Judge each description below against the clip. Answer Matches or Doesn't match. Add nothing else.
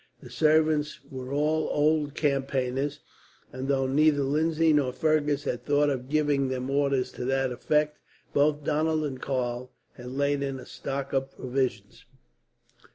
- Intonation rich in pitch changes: Doesn't match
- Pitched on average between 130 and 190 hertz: Matches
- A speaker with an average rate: Matches